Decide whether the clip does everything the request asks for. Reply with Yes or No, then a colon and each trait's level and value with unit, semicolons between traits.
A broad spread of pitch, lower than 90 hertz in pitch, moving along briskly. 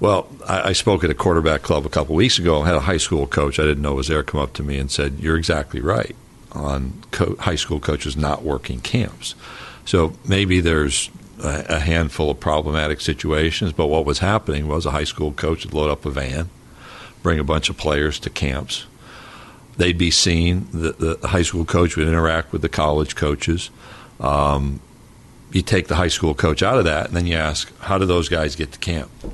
No: average, 2.8 semitones; very low, 80 Hz; fast, 215 wpm